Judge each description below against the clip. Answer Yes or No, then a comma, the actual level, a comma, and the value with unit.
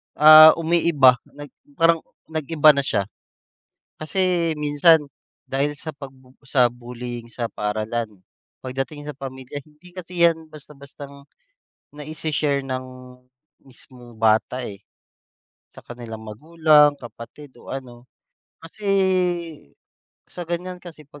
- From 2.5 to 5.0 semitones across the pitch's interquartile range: Yes, average, 4.1 semitones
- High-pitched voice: No, medium, 145 Hz